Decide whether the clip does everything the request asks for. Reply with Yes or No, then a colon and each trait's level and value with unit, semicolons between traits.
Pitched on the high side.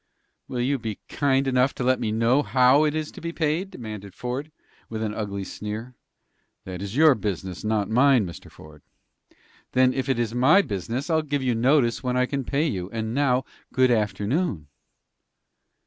No: low, 125 Hz